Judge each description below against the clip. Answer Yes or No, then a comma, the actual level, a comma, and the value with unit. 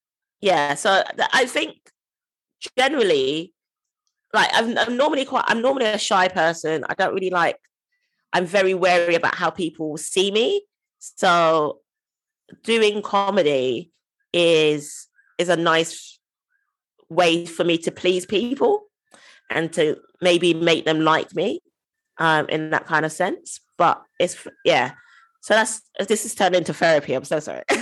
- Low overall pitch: No, high, 190 Hz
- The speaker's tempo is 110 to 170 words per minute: Yes, average, 140 wpm